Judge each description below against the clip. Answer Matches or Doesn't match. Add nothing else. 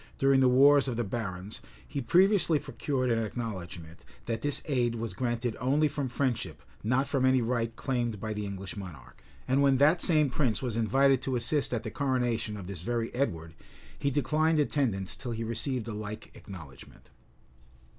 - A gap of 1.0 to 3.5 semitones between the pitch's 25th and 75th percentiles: Doesn't match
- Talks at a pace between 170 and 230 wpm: Matches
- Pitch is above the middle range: Doesn't match